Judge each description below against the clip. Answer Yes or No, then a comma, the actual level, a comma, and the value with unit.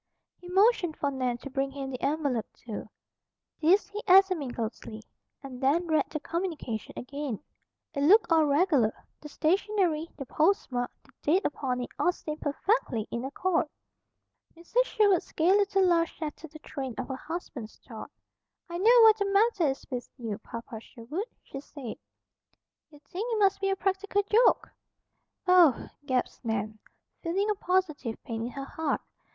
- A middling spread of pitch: No, wide, 6.5 semitones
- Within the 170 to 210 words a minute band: No, average, 160 wpm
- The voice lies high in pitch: Yes, very high, 310 Hz